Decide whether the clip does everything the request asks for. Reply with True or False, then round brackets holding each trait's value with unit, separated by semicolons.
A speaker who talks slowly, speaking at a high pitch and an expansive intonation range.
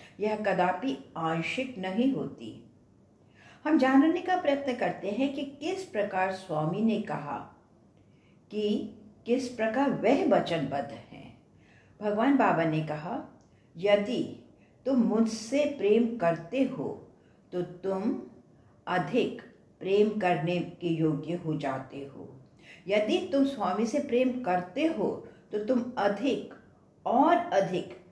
True (115 wpm; 215 Hz; 6.8 semitones)